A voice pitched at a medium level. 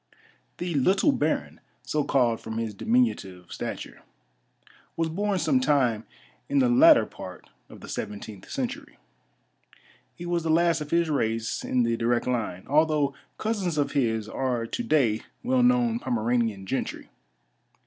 Yes: medium, 150 Hz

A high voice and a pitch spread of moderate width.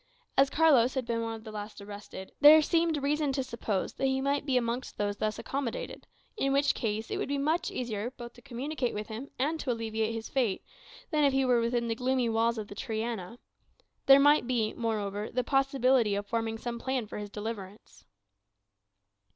Yes: high, 235 Hz; average, 3.7 semitones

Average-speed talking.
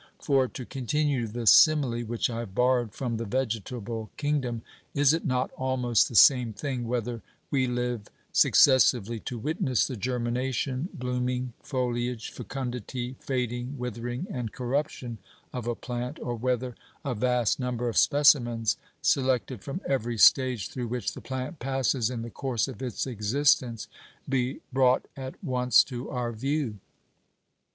Yes: average, 145 wpm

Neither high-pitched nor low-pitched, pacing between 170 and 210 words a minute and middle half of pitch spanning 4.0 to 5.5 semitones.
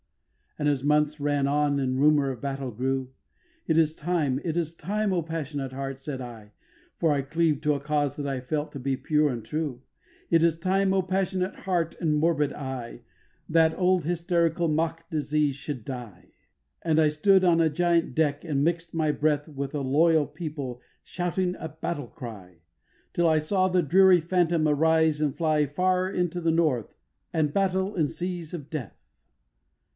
No: medium, 155 Hz; average, 180 wpm; average, 3.3 semitones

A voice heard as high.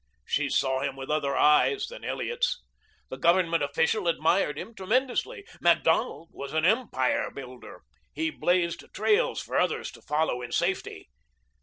No: medium, 165 Hz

